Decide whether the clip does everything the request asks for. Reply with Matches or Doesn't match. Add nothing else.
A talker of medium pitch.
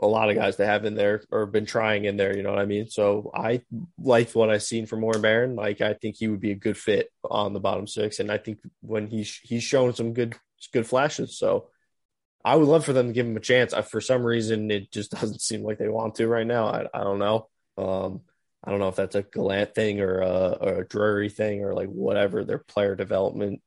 Doesn't match